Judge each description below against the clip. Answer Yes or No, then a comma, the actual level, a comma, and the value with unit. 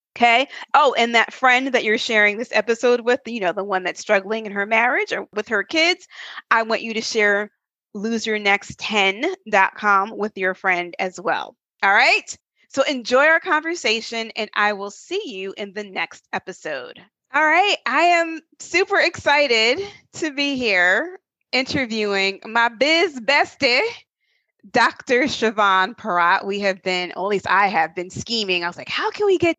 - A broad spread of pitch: Yes, wide, 6.2 semitones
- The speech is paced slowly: No, average, 170 wpm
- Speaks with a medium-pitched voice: No, high, 225 Hz